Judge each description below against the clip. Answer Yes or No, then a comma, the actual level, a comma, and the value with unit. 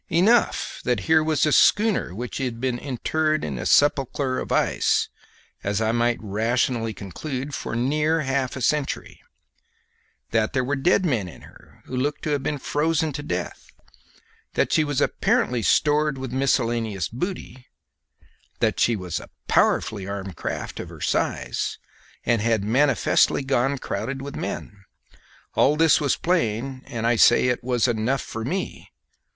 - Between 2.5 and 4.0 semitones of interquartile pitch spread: No, average, 4.4 semitones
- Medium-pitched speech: No, low, 130 Hz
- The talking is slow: No, average, 160 wpm